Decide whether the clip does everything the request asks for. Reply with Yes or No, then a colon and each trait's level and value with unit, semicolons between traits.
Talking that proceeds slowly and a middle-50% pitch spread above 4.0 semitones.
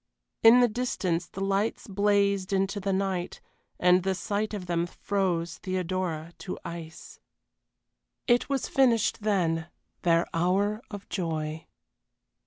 No: slow, 125 wpm; average, 3.0 semitones